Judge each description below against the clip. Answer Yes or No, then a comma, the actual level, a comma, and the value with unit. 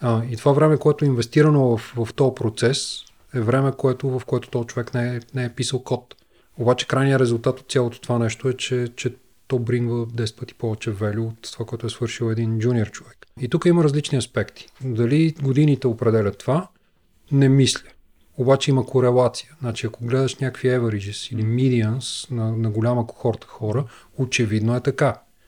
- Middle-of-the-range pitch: No, low, 125 Hz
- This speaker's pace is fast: Yes, fast, 180 wpm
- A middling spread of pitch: No, narrow, 2.3 semitones